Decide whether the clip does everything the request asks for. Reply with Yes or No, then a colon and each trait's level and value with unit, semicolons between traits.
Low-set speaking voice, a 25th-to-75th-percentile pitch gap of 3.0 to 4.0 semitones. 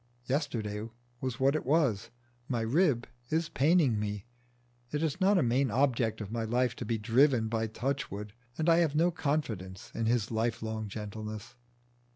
No: low, 120 Hz; average, 4.9 semitones